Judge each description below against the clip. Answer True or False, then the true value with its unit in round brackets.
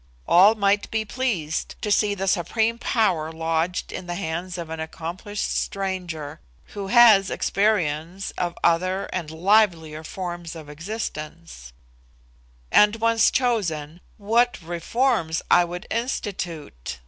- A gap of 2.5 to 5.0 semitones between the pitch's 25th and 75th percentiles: True (4.4 semitones)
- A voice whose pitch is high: False (180 Hz)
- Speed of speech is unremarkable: False (125 wpm)